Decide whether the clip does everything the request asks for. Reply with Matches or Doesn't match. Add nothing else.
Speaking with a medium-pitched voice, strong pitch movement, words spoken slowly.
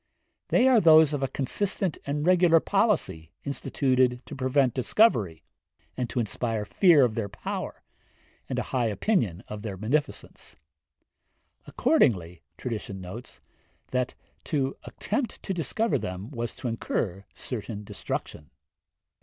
Doesn't match